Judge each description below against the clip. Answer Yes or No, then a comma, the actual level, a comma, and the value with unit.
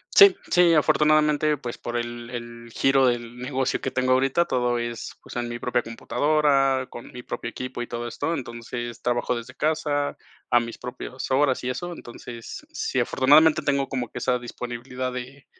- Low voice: Yes, low, 125 Hz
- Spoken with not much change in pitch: No, average, 3.2 semitones